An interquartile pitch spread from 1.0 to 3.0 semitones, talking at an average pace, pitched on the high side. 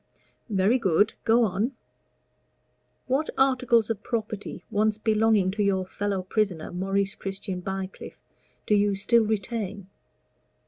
No: narrow, 2.5 semitones; slow, 120 wpm; high, 205 Hz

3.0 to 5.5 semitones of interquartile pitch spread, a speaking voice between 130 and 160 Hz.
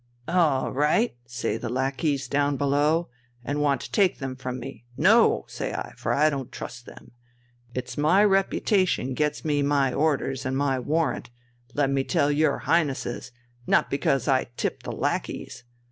No: narrow, 2.5 semitones; medium, 140 Hz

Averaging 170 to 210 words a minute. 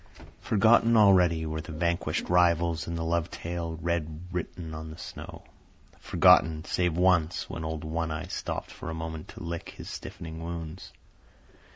No: average, 160 wpm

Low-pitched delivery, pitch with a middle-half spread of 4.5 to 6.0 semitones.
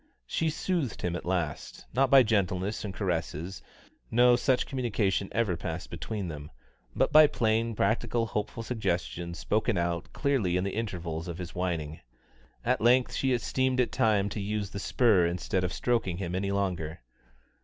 Yes: low, 100 Hz; average, 5.1 semitones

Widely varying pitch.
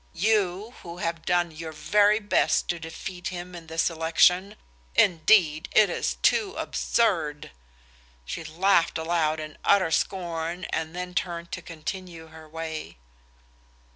No: narrow, 2.5 semitones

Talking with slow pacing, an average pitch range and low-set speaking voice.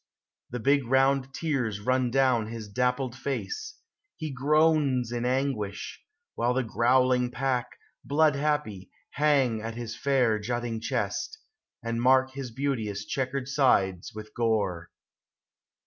Yes: slow, 125 wpm; average, 3.2 semitones; low, 125 Hz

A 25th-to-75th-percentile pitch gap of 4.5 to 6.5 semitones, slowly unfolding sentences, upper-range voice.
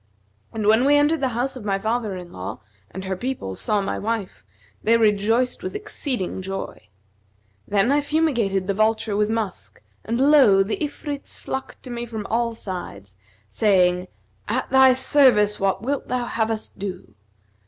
No: average, 4.8 semitones; average, 165 wpm; high, 225 Hz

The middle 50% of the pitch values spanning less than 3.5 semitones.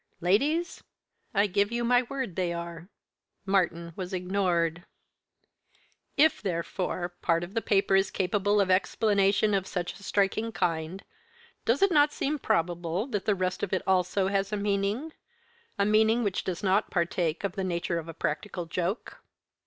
Yes: average, 3.0 semitones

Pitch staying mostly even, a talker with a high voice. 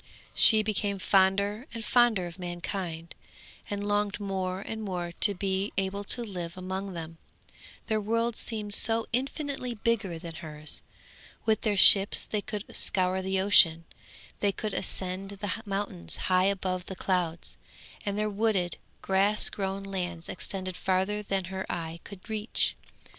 Yes: narrow, 2.3 semitones; high, 195 Hz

